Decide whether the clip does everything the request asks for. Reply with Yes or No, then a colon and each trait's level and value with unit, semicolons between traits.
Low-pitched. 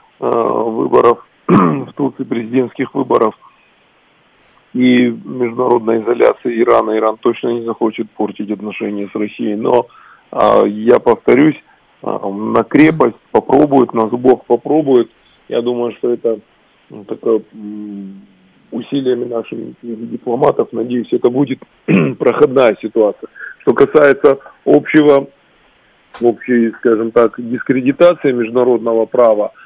Yes: low, 120 Hz